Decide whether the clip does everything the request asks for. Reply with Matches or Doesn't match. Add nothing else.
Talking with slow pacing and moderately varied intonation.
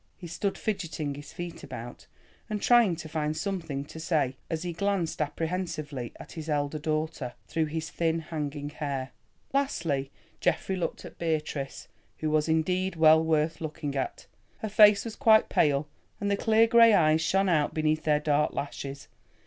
Doesn't match